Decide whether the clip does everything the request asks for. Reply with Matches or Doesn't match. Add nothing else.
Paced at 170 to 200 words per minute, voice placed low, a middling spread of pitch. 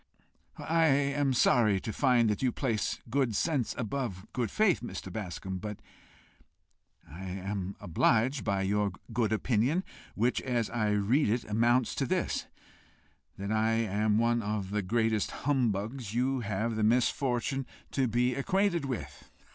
Doesn't match